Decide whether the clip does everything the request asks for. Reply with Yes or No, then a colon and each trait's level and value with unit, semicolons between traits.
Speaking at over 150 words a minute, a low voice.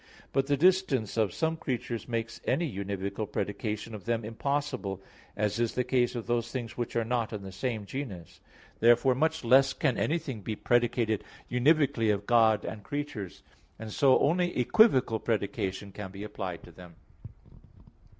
Yes: average, 160 wpm; low, 115 Hz